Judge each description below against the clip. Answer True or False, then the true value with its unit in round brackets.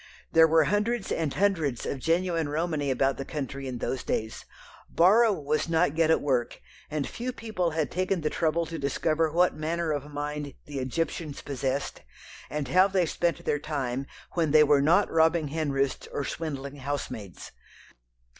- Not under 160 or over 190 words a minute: True (165 wpm)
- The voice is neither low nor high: True (155 Hz)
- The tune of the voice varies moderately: True (3.2 semitones)